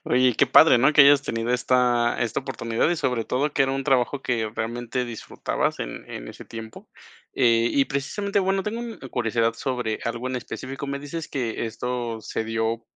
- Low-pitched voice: Yes, low, 125 Hz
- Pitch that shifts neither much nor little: Yes, average, 3.0 semitones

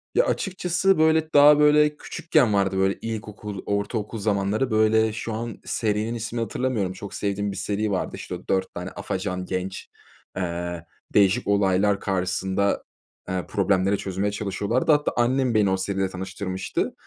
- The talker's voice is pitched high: No, low, 105 Hz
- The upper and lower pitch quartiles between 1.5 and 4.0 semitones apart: Yes, average, 3.5 semitones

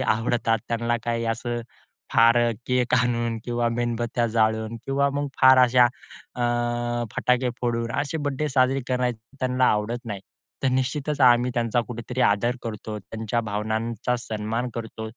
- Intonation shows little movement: Yes, narrow, 1.8 semitones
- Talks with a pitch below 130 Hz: Yes, low, 120 Hz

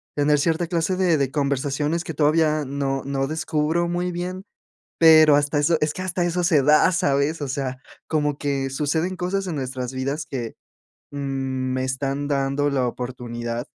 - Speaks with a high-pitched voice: No, medium, 145 Hz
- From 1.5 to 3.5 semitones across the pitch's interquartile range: Yes, average, 3.2 semitones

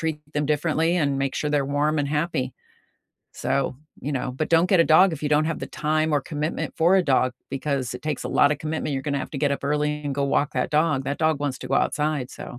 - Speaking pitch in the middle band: Yes, medium, 150 Hz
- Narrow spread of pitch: Yes, narrow, 2.0 semitones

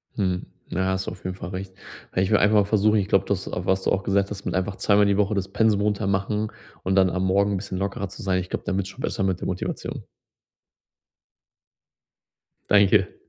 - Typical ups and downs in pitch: No, narrow, 1.4 semitones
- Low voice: Yes, very low, 95 Hz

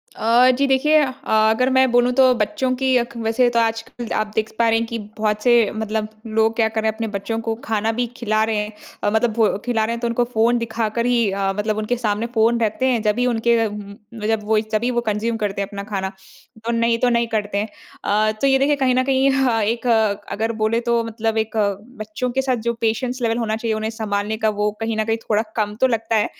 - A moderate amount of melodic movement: No, narrow, 1.8 semitones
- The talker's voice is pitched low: No, high, 225 Hz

